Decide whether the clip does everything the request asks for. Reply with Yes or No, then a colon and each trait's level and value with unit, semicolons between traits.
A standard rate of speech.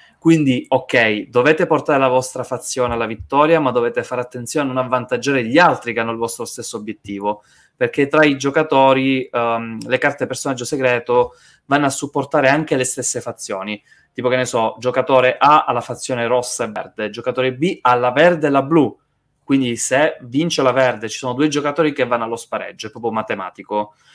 No: fast, 190 wpm